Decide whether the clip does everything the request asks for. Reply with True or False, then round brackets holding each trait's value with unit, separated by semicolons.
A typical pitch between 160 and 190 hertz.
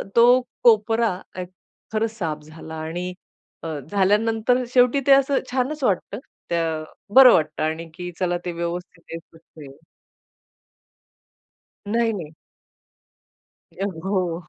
True (185 Hz)